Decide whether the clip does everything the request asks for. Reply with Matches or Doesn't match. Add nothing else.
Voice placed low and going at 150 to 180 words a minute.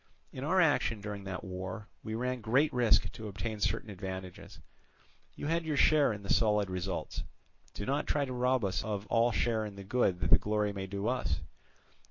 Doesn't match